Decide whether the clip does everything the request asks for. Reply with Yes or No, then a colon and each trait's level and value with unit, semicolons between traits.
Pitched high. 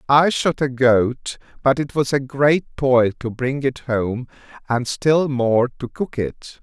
No: low, 130 Hz